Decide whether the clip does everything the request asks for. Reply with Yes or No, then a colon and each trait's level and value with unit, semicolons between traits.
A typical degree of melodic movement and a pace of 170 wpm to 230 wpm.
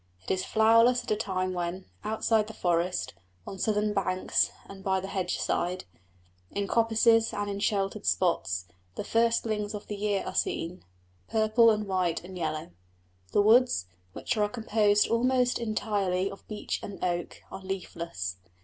No: average, 3.0 semitones; average, 160 wpm